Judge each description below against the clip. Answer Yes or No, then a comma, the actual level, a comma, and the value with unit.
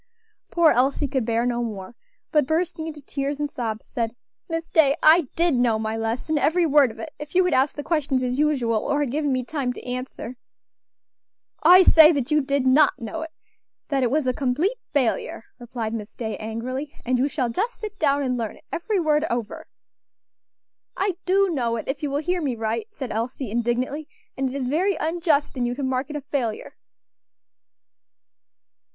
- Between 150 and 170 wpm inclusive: No, average, 195 wpm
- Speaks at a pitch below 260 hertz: No, very high, 275 Hz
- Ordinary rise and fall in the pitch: Yes, average, 4.3 semitones